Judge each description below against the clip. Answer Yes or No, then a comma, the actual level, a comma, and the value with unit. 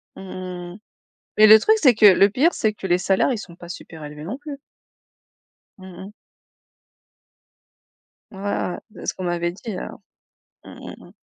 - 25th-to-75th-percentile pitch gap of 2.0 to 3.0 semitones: No, average, 3.6 semitones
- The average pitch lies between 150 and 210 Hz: Yes, high, 190 Hz